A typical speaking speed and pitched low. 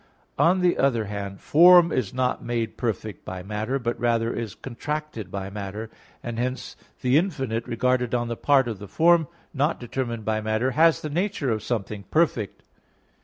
Yes: average, 170 wpm; low, 120 Hz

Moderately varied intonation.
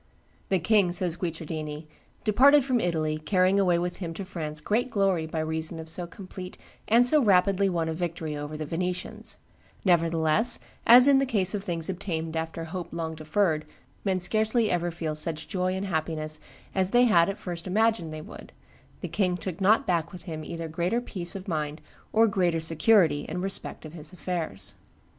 Yes: average, 3.6 semitones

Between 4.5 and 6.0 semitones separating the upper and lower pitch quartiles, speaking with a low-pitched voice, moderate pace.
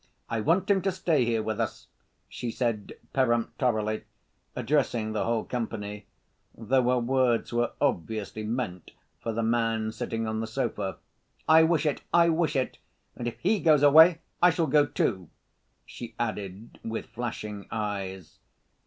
Yes: average, 4.8 semitones; low, 115 Hz; average, 155 wpm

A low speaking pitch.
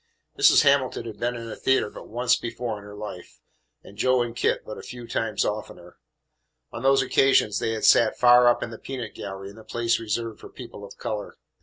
Yes: low, 115 Hz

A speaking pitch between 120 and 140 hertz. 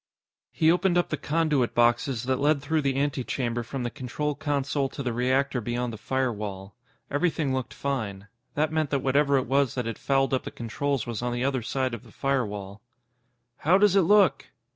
Yes: low, 135 Hz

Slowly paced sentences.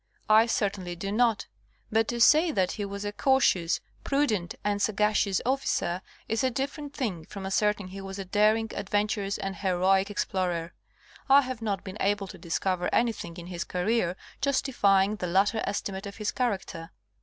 No: average, 165 wpm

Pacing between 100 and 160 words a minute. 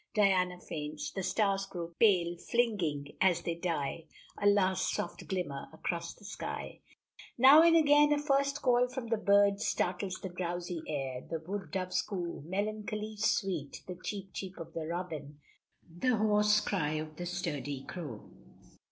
Yes: average, 155 wpm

